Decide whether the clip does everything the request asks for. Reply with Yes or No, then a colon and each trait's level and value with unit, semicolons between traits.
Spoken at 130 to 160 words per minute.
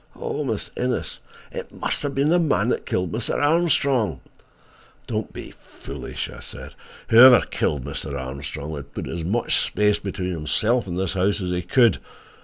No: average, 175 wpm